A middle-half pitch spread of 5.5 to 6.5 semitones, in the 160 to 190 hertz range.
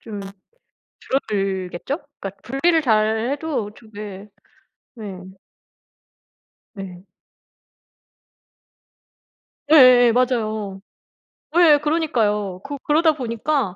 No: wide, 5.9 semitones; high, 225 Hz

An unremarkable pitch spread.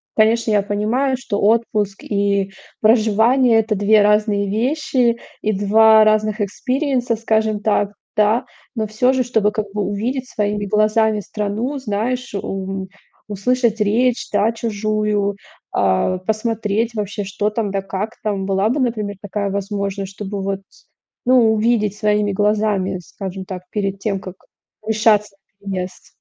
No: narrow, 2.0 semitones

